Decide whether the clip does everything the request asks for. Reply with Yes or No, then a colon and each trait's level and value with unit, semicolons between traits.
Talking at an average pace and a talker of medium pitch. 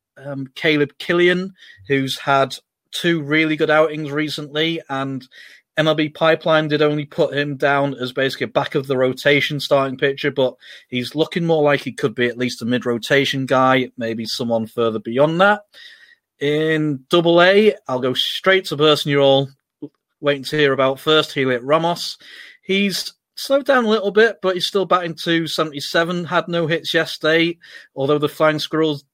Yes: average, 170 wpm; medium, 150 Hz